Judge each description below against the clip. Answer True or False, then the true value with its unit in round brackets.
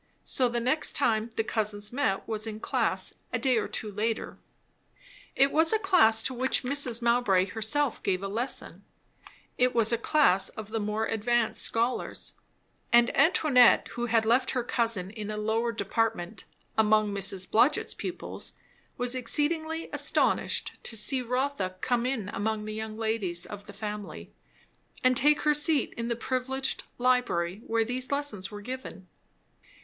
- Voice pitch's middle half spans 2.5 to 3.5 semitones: True (3.2 semitones)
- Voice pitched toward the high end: True (230 Hz)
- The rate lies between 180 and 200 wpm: False (160 wpm)